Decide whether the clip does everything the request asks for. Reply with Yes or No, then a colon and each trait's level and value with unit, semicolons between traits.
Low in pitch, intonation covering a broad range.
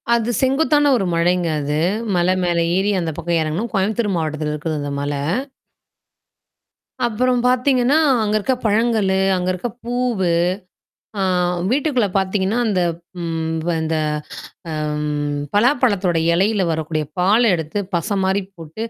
No: high, 195 Hz; wide, 6.1 semitones